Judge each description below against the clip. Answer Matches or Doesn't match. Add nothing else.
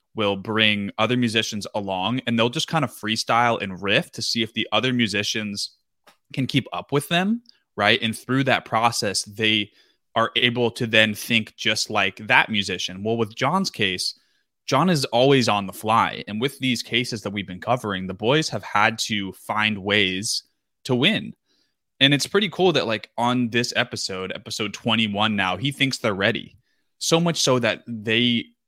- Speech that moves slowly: Doesn't match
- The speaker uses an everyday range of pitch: Matches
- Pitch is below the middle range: Matches